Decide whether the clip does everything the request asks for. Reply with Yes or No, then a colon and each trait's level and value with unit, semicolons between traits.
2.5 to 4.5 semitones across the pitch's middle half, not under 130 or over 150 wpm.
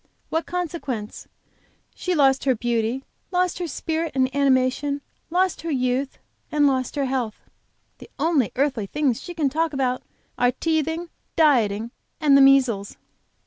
Yes: average, 4.1 semitones; average, 145 wpm